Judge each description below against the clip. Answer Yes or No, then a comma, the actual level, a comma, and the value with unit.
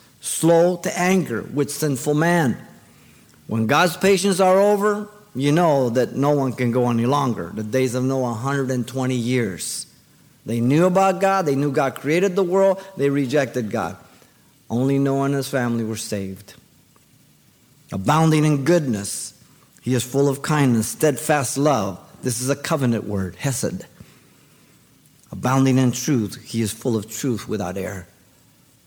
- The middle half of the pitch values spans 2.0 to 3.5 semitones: No, average, 4.2 semitones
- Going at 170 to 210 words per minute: No, average, 150 wpm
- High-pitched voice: No, low, 135 Hz